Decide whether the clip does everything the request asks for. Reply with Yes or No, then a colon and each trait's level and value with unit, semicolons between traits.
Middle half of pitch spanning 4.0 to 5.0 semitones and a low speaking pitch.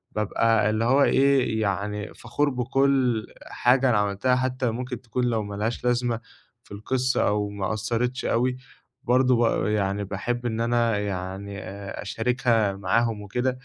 No: average, 3.3 semitones; low, 115 Hz